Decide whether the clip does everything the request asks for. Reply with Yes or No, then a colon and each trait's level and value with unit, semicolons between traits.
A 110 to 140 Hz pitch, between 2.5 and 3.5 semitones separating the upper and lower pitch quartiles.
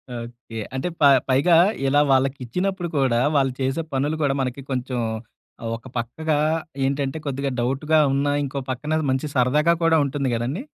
Yes: low, 135 Hz; average, 2.8 semitones